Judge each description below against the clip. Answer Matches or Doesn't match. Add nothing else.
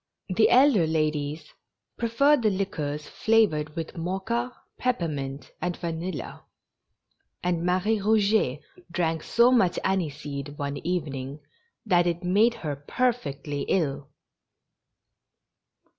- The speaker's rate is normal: Doesn't match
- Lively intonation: Matches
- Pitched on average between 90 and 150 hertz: Doesn't match